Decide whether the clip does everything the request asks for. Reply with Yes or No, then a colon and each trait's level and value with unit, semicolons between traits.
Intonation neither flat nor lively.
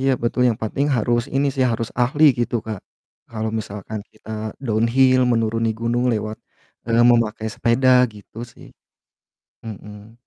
No: narrow, 2.2 semitones